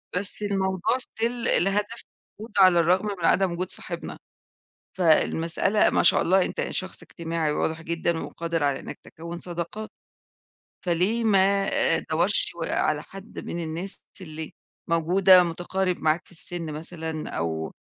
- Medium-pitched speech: Yes, medium, 175 Hz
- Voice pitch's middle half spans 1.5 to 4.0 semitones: Yes, average, 2.9 semitones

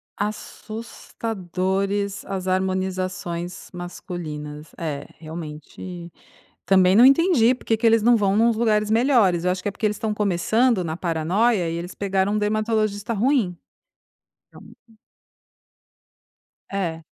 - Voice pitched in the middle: No, high, 195 Hz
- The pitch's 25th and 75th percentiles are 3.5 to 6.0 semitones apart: Yes, average, 3.8 semitones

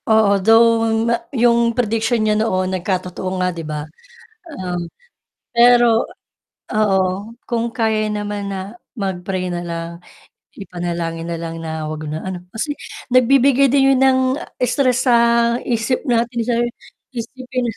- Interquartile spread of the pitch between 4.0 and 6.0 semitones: Yes, average, 4.8 semitones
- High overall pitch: Yes, high, 215 Hz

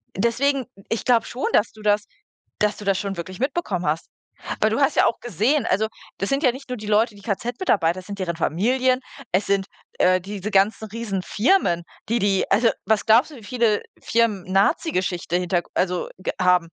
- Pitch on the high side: Yes, high, 210 Hz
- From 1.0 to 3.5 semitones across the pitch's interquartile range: No, average, 4.0 semitones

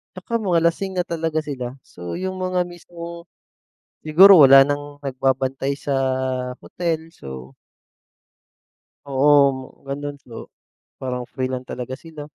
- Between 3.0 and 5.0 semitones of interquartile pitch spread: Yes, average, 4.5 semitones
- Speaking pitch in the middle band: Yes, medium, 145 Hz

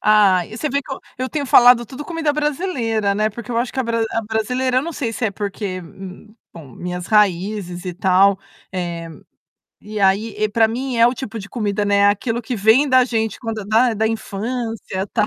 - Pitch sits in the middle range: No, high, 220 Hz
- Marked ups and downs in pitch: No, average, 3.6 semitones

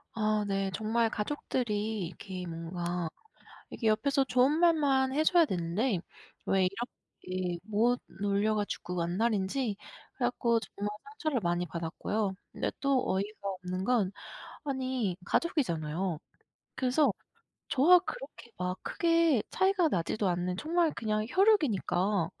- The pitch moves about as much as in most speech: No, wide, 6.3 semitones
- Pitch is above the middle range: Yes, high, 215 Hz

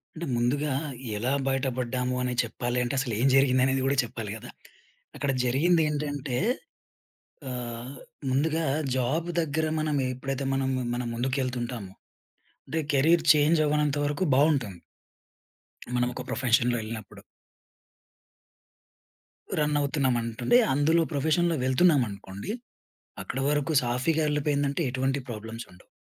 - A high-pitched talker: No, low, 135 Hz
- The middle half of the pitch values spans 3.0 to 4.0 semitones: Yes, average, 3.4 semitones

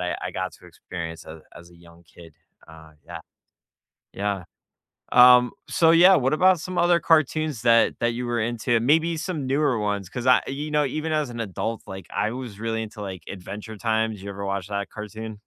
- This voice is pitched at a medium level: No, low, 115 Hz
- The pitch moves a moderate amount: No, wide, 6.4 semitones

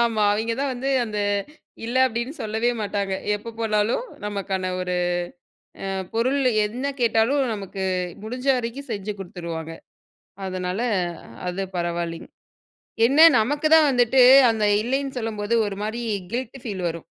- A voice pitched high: Yes, high, 220 Hz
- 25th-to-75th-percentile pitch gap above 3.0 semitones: Yes, average, 4.0 semitones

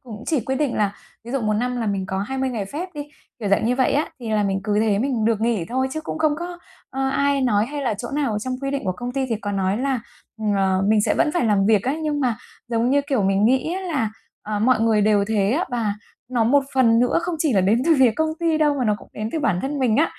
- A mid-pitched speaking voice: No, high, 240 Hz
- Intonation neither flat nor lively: Yes, average, 4.7 semitones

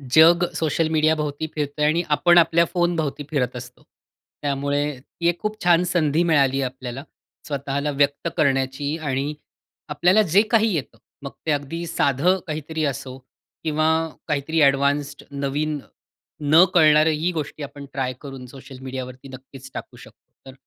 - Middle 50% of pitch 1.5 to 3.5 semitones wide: Yes, average, 2.9 semitones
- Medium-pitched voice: Yes, medium, 145 Hz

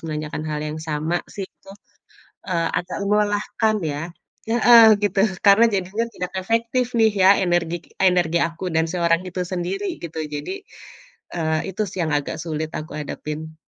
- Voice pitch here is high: No, medium, 175 Hz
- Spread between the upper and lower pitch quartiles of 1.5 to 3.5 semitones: No, average, 4.5 semitones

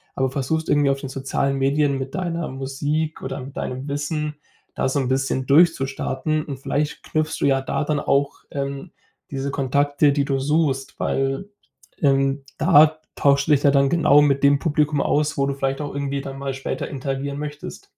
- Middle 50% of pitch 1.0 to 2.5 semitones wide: Yes, narrow, 1.7 semitones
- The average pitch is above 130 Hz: Yes, medium, 140 Hz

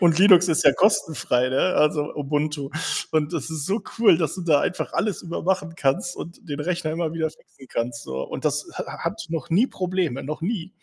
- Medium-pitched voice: Yes, medium, 160 Hz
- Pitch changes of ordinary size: Yes, average, 3.5 semitones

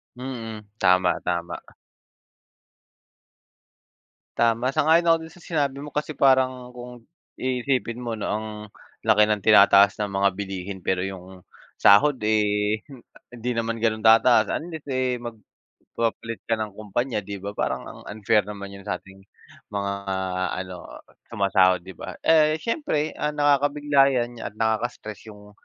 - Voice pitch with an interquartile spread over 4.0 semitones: Yes, average, 4.4 semitones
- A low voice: Yes, low, 115 Hz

